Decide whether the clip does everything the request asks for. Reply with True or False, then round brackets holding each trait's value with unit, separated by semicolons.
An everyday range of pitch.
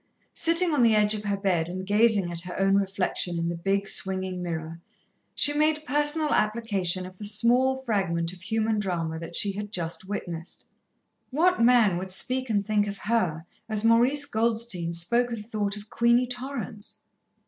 True (4.4 semitones)